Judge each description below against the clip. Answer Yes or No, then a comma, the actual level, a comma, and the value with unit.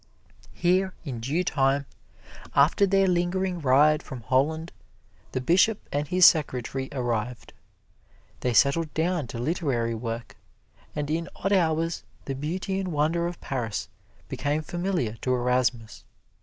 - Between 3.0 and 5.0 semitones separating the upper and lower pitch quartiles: No, wide, 5.4 semitones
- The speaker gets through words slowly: Yes, slow, 130 wpm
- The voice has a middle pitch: Yes, medium, 150 Hz